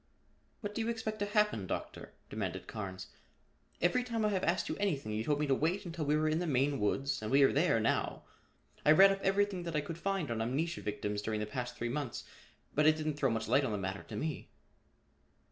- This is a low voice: No, medium, 150 Hz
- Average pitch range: No, wide, 8.2 semitones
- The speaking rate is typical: No, fast, 230 wpm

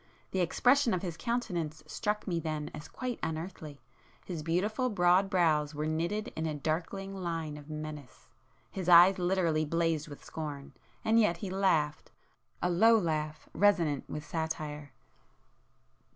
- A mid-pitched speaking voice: Yes, medium, 165 Hz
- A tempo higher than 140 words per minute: No, slow, 135 wpm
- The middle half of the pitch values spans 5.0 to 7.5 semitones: No, average, 3.9 semitones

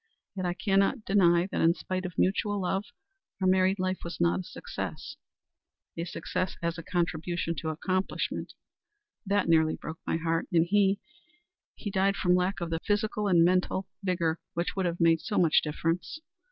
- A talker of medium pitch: Yes, medium, 180 Hz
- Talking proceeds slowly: No, average, 175 wpm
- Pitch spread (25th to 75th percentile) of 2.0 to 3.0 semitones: Yes, narrow, 2.5 semitones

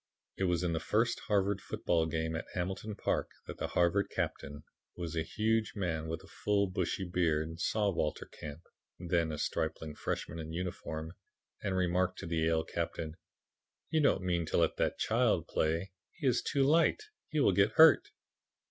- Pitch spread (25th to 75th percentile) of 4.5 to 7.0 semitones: No, average, 3.5 semitones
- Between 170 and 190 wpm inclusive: Yes, average, 180 wpm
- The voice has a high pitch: No, very low, 85 Hz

